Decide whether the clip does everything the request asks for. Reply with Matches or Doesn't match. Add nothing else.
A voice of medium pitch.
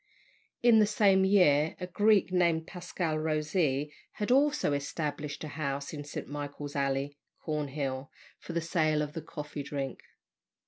Matches